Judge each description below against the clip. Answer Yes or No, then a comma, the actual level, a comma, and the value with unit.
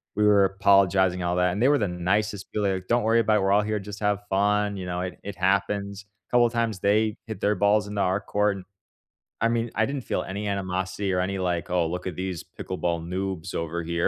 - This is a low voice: Yes, low, 100 Hz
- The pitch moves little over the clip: Yes, narrow, 2.3 semitones